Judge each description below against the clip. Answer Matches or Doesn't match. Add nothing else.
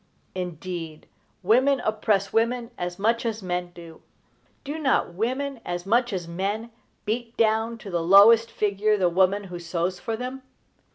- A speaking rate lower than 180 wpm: Matches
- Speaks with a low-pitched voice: Doesn't match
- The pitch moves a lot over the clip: Doesn't match